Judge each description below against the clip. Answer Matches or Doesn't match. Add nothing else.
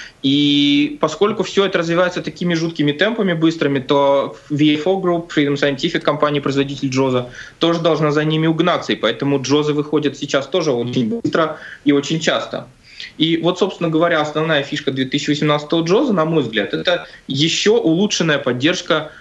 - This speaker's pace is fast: Doesn't match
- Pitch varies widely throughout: Doesn't match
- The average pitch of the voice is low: Doesn't match